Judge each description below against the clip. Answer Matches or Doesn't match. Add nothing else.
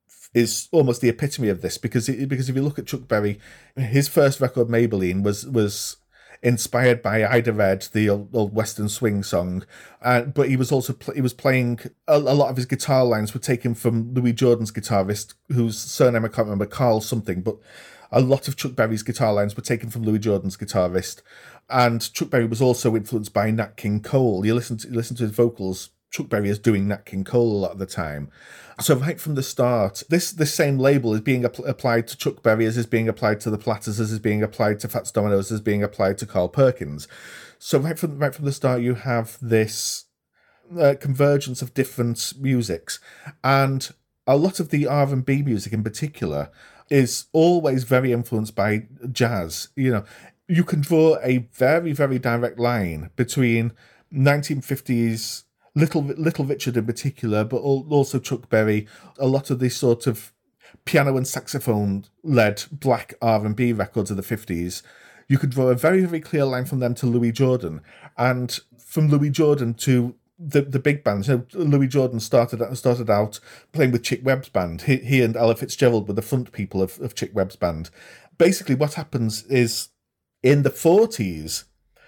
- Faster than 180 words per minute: Matches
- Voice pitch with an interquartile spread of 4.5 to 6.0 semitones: Doesn't match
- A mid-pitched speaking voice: Doesn't match